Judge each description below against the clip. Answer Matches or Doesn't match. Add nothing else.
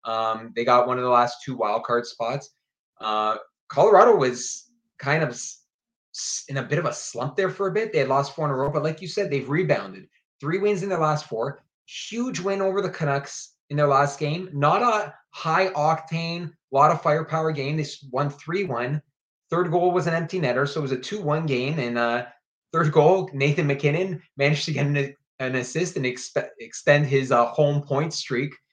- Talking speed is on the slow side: Doesn't match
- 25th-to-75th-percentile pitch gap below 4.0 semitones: Doesn't match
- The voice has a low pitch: Doesn't match